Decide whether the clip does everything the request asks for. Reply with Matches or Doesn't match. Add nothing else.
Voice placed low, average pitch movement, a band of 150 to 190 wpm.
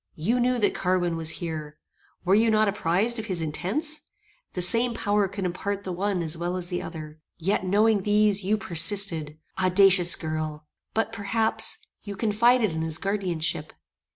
Doesn't match